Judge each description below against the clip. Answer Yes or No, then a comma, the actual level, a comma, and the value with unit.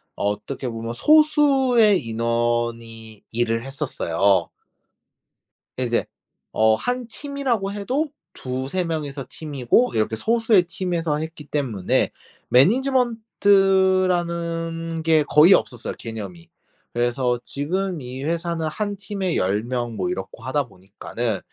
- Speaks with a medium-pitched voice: Yes, medium, 145 Hz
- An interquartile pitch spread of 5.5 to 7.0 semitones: No, wide, 8.4 semitones